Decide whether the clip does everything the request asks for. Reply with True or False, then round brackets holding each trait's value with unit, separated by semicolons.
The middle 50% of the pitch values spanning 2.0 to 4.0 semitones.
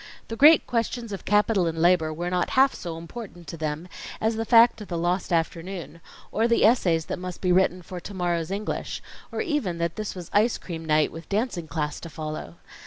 False (4.6 semitones)